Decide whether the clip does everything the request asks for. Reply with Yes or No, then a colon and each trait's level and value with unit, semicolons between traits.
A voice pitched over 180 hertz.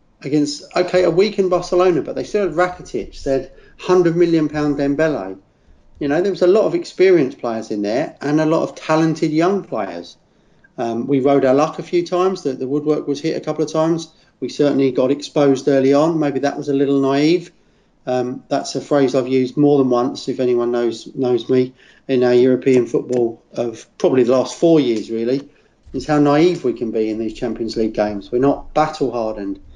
No: medium, 140 Hz